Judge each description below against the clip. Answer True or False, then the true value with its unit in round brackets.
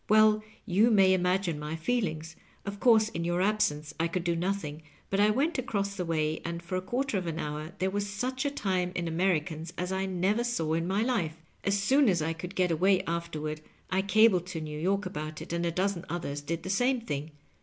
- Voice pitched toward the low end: False (185 Hz)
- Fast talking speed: True (220 wpm)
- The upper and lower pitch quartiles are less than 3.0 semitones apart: False (3.7 semitones)